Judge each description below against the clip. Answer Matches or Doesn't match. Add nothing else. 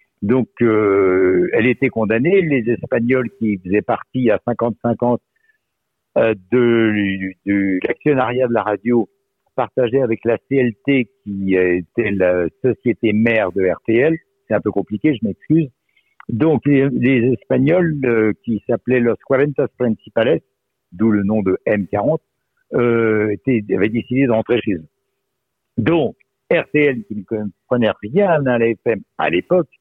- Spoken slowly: Matches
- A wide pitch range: Doesn't match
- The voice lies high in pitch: Doesn't match